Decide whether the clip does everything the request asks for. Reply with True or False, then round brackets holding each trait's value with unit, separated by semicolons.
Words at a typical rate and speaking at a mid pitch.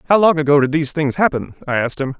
False (275 wpm; 150 Hz)